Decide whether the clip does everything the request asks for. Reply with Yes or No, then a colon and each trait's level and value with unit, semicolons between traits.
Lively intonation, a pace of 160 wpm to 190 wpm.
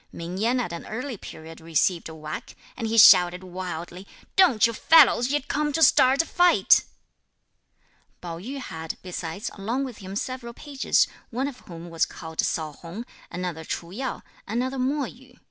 Yes: wide, 7.2 semitones; average, 170 wpm